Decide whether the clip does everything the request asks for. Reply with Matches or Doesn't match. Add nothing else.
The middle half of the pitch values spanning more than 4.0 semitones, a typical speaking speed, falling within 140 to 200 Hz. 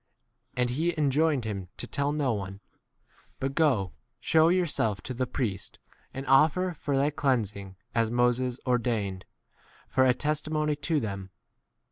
Doesn't match